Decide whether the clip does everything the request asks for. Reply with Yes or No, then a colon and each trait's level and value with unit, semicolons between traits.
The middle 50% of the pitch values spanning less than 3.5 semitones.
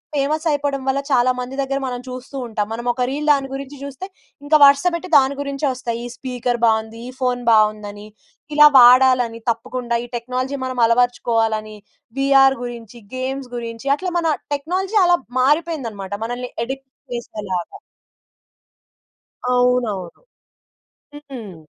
Yes: average, 3.1 semitones